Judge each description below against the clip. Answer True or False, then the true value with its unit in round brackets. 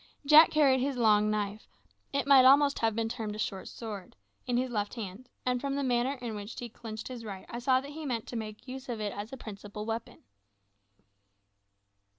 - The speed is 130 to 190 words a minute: False (205 wpm)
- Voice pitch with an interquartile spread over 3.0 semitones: True (3.6 semitones)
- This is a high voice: True (235 Hz)